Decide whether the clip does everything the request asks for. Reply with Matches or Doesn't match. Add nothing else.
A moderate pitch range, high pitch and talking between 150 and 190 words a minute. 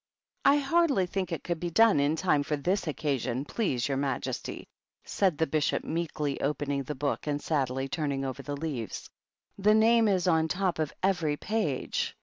Doesn't match